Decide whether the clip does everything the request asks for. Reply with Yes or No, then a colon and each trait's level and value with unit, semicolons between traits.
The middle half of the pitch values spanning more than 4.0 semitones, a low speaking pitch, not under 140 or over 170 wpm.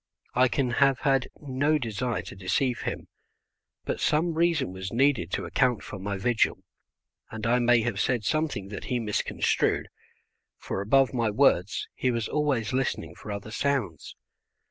Yes: average, 4.7 semitones; low, 120 Hz; average, 160 wpm